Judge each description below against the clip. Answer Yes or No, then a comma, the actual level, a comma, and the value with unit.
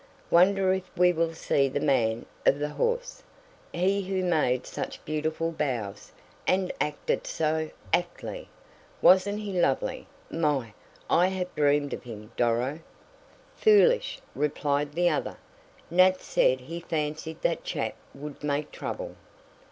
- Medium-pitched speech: Yes, medium, 160 Hz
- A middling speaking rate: No, slow, 130 wpm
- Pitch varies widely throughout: No, average, 4.4 semitones